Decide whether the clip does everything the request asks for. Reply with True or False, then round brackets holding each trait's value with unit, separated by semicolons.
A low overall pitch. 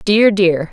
False (190 Hz)